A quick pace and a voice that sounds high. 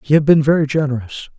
No: fast, 215 wpm; medium, 145 Hz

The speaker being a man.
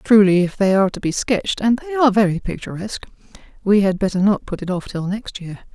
No: female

